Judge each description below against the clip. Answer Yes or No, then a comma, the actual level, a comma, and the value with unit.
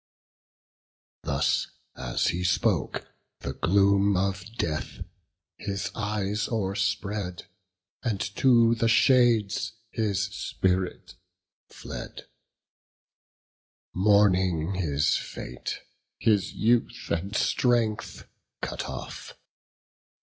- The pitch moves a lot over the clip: No, average, 2.8 semitones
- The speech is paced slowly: Yes, slow, 80 wpm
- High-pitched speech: No, low, 100 Hz